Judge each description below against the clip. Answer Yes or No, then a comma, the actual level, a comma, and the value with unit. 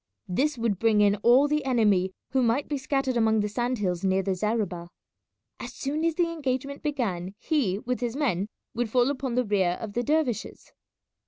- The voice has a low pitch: No, high, 235 Hz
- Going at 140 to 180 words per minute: No, average, 190 wpm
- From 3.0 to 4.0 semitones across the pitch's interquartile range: No, average, 5.0 semitones